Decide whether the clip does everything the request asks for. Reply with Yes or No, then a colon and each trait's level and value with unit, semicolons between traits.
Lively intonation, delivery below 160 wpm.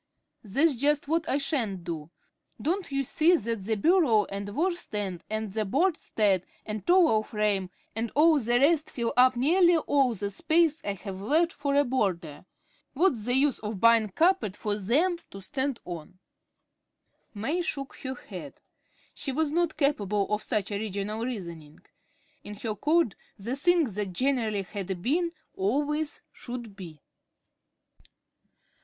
Yes: wide, 6.7 semitones; average, 150 wpm